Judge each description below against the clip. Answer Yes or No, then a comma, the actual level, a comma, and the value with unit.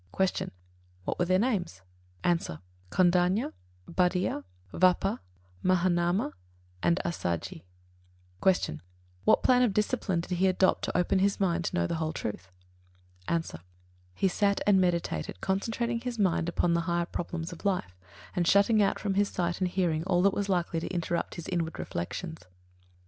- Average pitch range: No, narrow, 2.3 semitones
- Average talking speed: Yes, average, 160 wpm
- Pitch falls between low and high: Yes, medium, 180 Hz